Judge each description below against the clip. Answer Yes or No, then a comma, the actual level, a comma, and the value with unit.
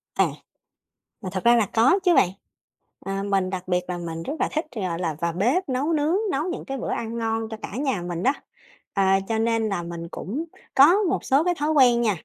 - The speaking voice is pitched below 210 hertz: No, high, 225 Hz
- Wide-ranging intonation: Yes, wide, 6.7 semitones